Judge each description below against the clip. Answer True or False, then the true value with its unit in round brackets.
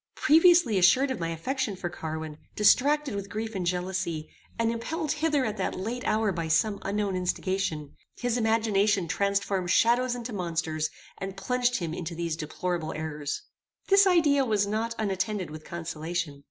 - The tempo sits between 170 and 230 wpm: False (155 wpm)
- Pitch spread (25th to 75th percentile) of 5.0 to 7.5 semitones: True (5.6 semitones)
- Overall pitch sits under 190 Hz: False (200 Hz)